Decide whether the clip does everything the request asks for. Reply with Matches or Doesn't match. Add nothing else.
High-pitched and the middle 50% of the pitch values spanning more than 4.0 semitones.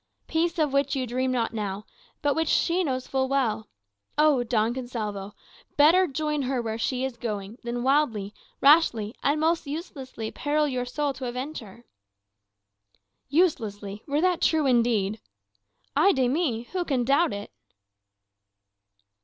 Matches